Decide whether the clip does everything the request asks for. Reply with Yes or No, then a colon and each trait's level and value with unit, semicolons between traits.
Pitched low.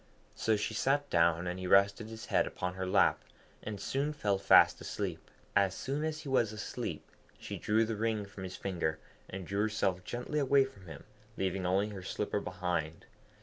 Yes: low, 100 Hz